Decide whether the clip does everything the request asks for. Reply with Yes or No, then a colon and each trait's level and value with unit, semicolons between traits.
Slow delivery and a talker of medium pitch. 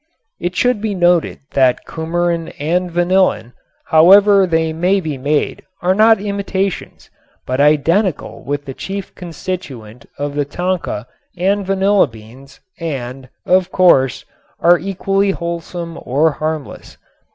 Yes: slow, 125 wpm; medium, 170 Hz